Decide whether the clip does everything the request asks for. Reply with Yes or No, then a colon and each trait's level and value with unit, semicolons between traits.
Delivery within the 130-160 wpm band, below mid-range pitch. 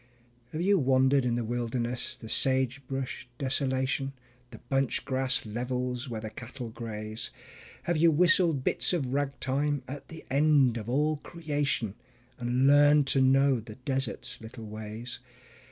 Yes: average, 145 wpm; low, 130 Hz